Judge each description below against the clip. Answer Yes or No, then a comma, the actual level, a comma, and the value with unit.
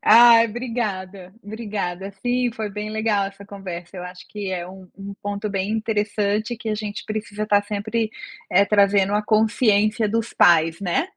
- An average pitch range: No, narrow, 1.8 semitones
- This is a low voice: No, high, 205 Hz